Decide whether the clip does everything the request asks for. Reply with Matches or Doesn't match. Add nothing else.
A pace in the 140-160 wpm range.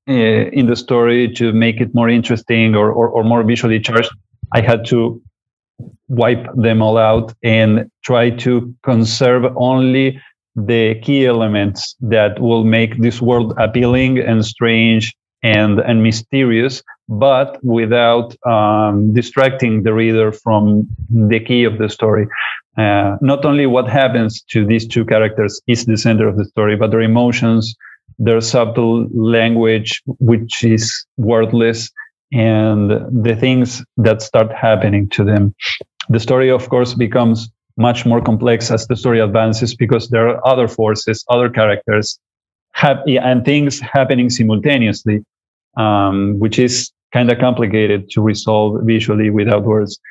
Matches